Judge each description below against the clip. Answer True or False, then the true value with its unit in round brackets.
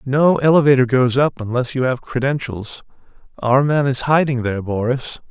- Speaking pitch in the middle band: False (130 Hz)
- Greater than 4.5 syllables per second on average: True (5.0 syllables/s)